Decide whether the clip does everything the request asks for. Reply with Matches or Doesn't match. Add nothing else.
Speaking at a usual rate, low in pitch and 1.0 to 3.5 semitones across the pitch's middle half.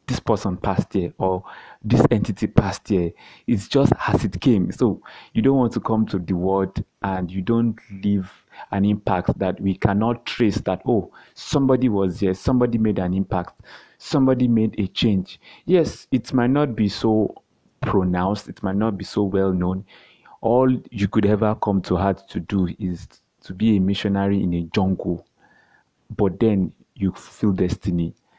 Matches